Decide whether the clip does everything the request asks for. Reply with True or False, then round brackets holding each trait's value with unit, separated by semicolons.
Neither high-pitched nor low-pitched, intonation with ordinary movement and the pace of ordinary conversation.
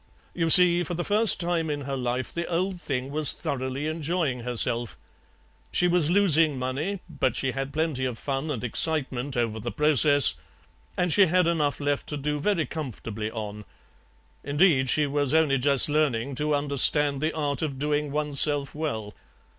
True (145 Hz; 3.5 semitones; 170 wpm)